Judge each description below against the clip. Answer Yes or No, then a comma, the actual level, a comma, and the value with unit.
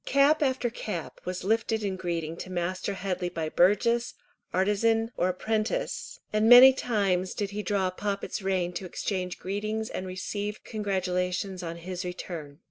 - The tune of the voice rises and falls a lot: No, average, 3.2 semitones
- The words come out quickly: No, average, 150 wpm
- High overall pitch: Yes, high, 195 Hz